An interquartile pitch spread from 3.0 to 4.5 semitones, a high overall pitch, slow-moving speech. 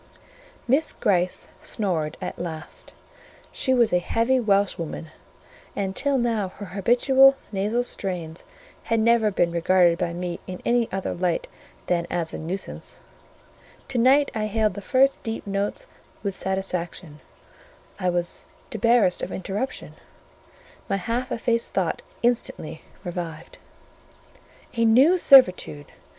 No: average, 5.0 semitones; high, 200 Hz; slow, 125 wpm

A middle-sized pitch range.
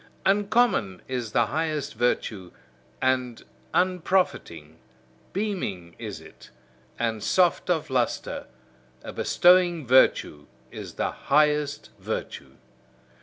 No: wide, 8.3 semitones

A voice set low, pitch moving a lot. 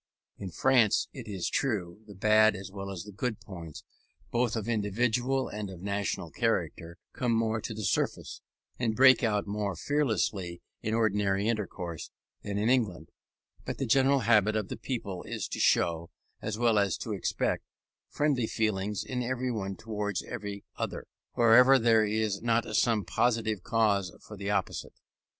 No: low, 110 Hz; average, 3.0 semitones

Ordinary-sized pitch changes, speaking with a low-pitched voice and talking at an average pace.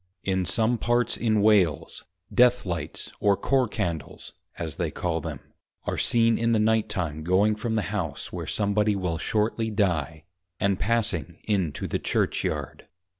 Yes: average, 3.9 semitones; low, 105 Hz; average, 170 wpm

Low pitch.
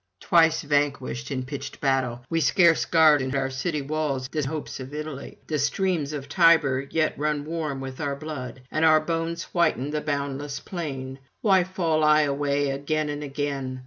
No: medium, 145 Hz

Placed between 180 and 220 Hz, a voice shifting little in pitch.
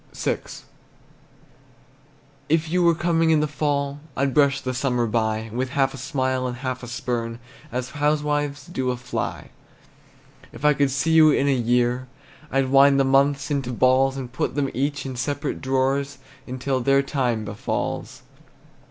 No: low, 135 Hz; narrow, 2.2 semitones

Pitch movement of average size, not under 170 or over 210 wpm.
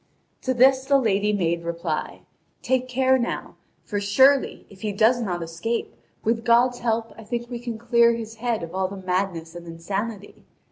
Yes: average, 4.3 semitones; average, 180 wpm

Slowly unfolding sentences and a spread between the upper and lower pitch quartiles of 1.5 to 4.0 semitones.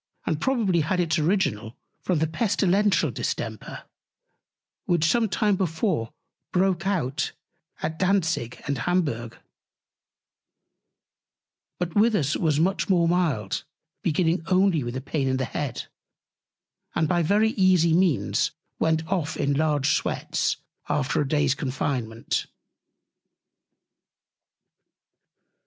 No: slow, 110 wpm; average, 4.7 semitones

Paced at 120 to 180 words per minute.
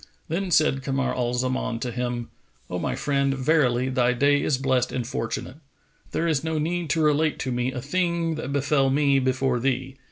No: average, 190 wpm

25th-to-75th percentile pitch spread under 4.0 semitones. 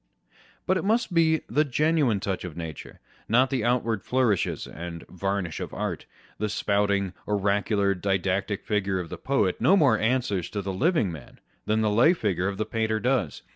No: average, 4.9 semitones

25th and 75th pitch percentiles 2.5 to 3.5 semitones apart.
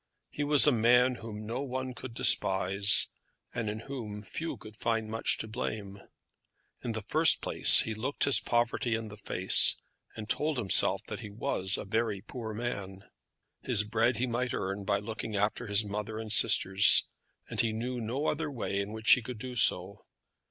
Yes: average, 3.0 semitones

